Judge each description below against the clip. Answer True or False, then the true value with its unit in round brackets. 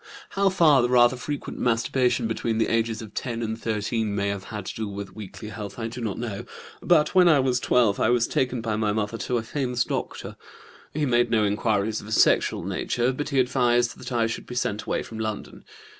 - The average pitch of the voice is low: True (115 Hz)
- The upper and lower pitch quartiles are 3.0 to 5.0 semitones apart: False (2.5 semitones)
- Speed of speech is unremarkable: False (220 wpm)